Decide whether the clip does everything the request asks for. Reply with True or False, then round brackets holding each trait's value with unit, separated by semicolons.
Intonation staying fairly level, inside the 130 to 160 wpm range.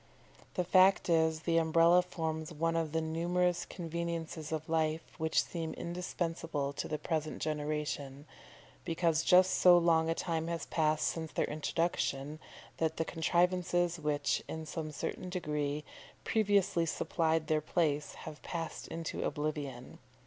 True (1.8 semitones; 140 wpm)